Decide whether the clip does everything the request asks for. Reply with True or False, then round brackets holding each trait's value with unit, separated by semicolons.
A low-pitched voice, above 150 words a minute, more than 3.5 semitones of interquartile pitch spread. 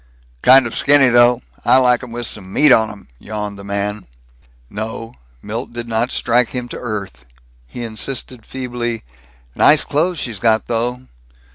False (120 Hz; 160 wpm; 2.6 semitones)